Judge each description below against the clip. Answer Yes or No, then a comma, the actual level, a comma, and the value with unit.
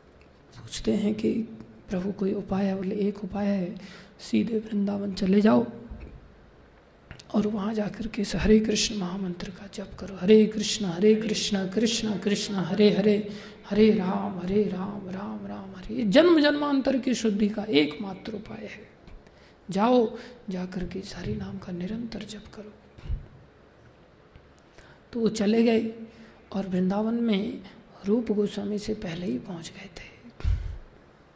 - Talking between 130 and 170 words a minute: Yes, average, 140 wpm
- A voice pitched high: Yes, high, 205 Hz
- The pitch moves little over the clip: Yes, narrow, 2.2 semitones